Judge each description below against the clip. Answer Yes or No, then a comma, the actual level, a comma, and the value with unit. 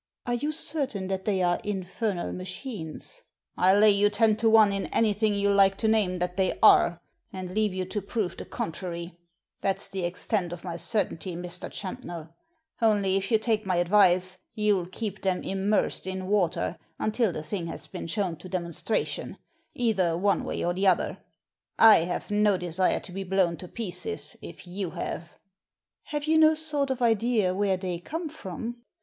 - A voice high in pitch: Yes, high, 195 Hz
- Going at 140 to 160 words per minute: No, average, 180 wpm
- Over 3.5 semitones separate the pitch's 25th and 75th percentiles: No, average, 3.2 semitones